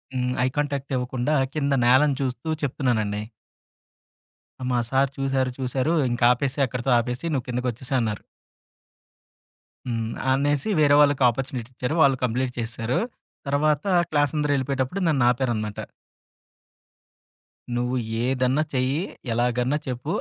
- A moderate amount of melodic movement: No, narrow, 2.3 semitones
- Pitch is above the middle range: No, low, 130 Hz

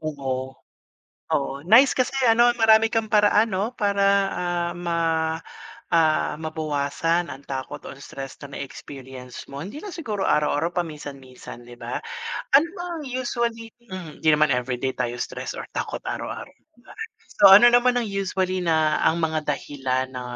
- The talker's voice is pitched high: No, medium, 165 Hz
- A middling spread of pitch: No, wide, 7.6 semitones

